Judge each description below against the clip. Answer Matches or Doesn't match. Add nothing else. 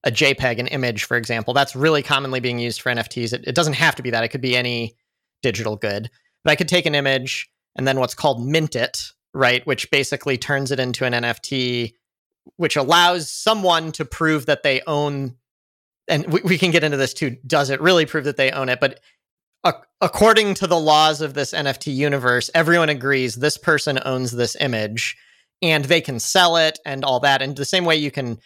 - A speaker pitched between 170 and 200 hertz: Doesn't match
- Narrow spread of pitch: Doesn't match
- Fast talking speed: Matches